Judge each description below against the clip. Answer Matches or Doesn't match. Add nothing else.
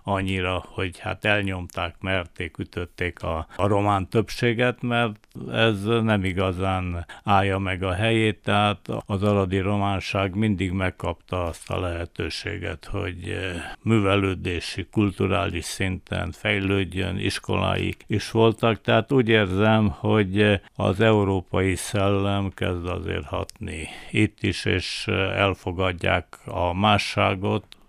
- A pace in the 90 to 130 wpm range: Matches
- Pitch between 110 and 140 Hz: Doesn't match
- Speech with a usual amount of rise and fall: Doesn't match